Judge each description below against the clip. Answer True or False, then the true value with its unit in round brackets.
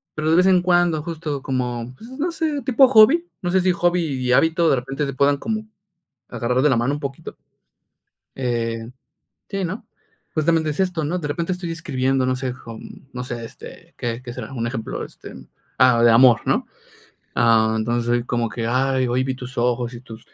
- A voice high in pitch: False (135 Hz)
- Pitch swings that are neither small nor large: False (6.0 semitones)